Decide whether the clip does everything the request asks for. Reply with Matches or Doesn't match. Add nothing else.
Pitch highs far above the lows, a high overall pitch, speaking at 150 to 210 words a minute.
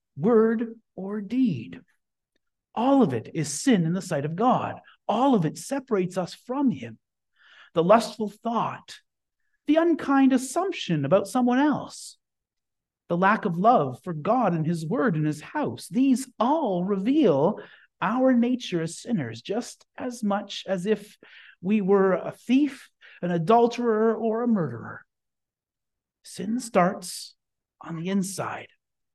Doesn't match